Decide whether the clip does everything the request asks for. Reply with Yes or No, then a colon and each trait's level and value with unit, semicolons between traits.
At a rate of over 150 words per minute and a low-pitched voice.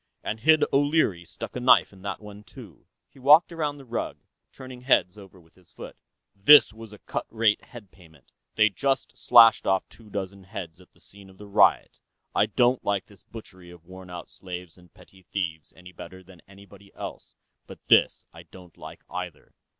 Yes: average, 190 wpm; low, 100 Hz